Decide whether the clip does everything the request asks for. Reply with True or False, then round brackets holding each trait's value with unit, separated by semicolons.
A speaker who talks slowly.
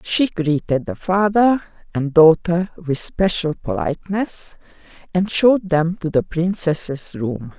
True (125 wpm)